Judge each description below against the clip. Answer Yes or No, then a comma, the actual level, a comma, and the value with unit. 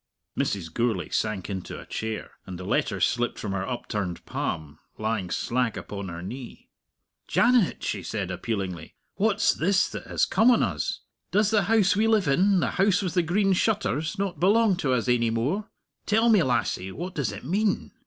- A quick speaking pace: No, average, 185 wpm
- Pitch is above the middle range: No, low, 135 Hz